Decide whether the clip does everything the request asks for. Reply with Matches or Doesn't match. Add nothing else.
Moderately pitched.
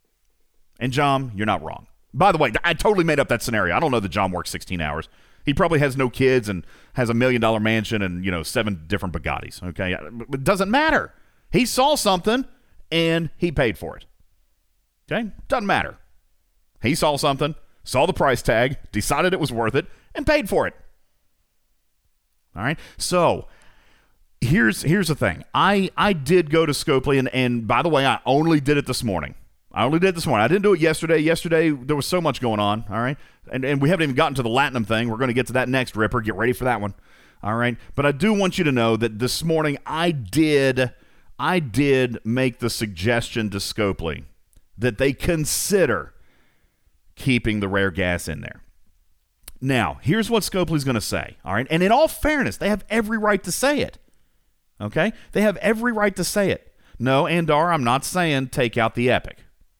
Doesn't match